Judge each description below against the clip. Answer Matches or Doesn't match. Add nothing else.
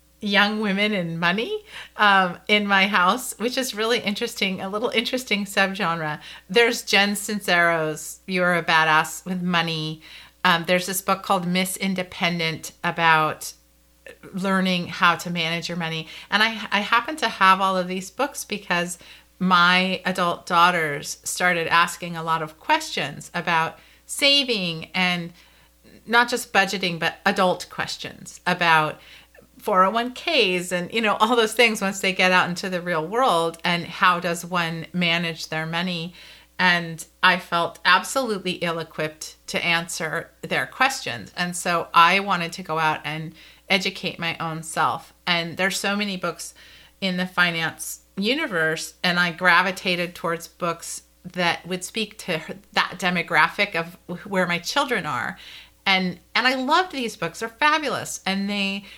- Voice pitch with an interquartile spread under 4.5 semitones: Matches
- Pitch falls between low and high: Matches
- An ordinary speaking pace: Matches